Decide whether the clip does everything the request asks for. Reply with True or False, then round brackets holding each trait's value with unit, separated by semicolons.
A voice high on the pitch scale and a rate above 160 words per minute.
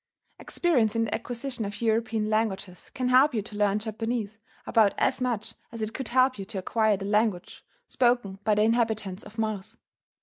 True (220 Hz; 180 wpm)